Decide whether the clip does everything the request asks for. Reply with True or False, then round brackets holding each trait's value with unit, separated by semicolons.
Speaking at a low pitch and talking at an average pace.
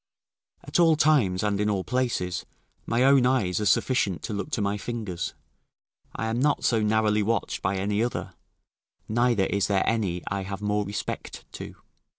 True (105 Hz; 170 wpm)